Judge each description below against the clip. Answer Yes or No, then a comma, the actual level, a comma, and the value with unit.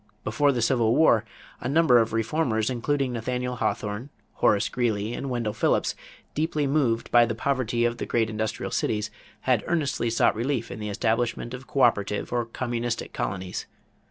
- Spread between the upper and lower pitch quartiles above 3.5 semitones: No, average, 2.7 semitones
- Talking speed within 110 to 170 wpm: Yes, average, 160 wpm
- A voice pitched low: Yes, low, 120 Hz